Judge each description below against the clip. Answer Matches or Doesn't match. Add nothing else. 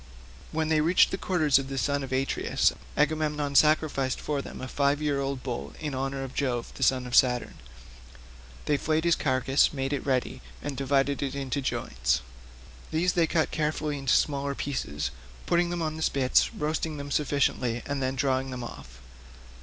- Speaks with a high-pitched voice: Doesn't match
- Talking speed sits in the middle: Matches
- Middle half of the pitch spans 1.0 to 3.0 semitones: Matches